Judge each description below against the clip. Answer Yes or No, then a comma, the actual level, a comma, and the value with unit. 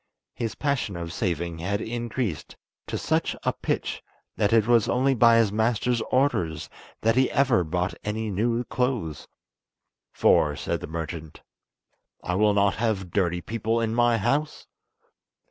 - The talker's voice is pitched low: Yes, low, 110 Hz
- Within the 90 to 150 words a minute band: Yes, average, 145 wpm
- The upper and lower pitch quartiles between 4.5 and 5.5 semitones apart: Yes, average, 5.0 semitones